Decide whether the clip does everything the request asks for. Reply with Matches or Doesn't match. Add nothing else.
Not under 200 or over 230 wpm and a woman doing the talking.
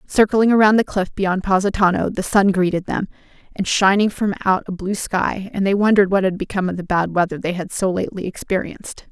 Matches